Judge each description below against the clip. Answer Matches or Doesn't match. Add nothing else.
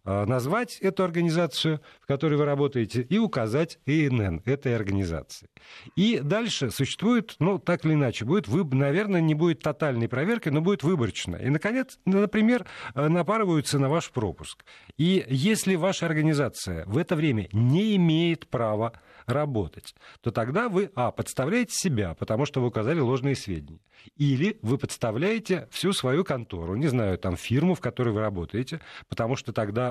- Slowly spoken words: Doesn't match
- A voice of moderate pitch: Matches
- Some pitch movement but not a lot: Doesn't match